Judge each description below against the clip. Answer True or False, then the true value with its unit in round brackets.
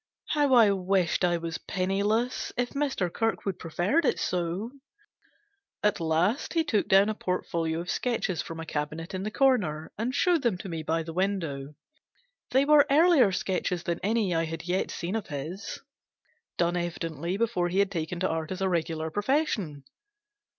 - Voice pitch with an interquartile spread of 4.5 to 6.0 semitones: True (5.2 semitones)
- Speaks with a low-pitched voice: False (185 Hz)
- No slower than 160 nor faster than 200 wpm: True (170 wpm)